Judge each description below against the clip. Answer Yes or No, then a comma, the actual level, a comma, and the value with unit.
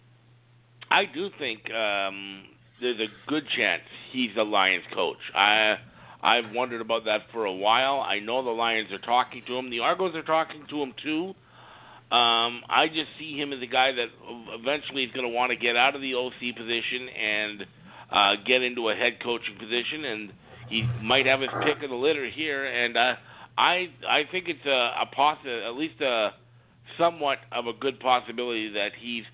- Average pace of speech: Yes, average, 190 wpm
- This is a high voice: No, low, 120 Hz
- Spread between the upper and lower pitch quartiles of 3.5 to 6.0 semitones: No, average, 3.1 semitones